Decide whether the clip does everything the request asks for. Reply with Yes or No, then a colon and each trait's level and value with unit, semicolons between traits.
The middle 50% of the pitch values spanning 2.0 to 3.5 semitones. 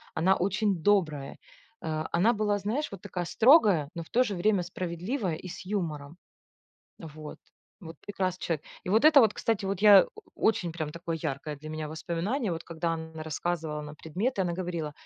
No: average, 4.3 semitones